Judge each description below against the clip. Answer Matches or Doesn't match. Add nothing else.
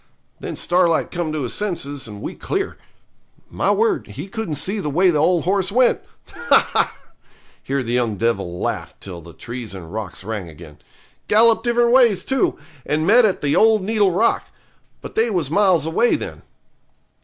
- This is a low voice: Doesn't match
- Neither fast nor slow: Matches